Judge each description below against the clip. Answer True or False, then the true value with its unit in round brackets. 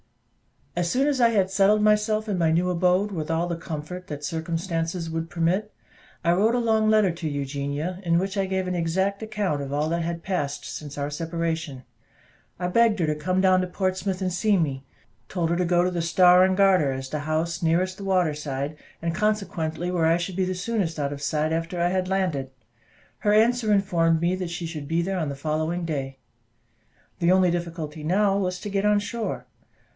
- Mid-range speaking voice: True (175 Hz)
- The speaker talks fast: True (210 wpm)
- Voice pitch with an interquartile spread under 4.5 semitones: True (3.0 semitones)